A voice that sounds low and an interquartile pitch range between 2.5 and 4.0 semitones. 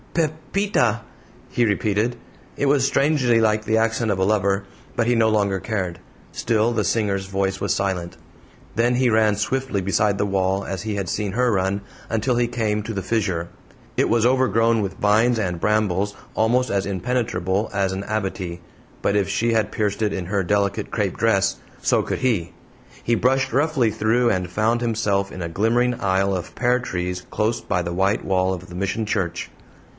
Yes: low, 105 Hz; average, 3.3 semitones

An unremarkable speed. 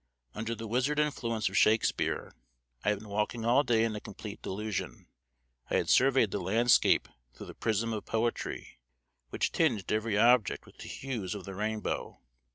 Yes: average, 170 wpm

